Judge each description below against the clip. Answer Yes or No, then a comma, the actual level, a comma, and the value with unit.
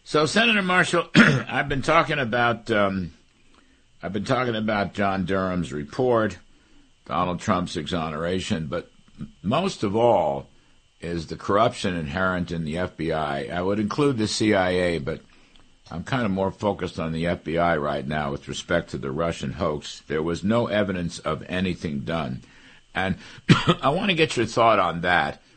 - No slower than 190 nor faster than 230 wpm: No, average, 155 wpm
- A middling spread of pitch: No, wide, 5.7 semitones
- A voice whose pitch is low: Yes, very low, 95 Hz